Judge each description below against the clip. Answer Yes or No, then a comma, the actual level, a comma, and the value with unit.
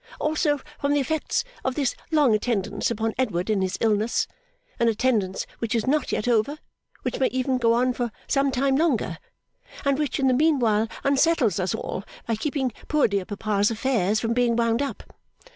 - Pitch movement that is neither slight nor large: Yes, average, 4.2 semitones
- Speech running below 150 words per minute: No, average, 180 wpm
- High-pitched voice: Yes, high, 240 Hz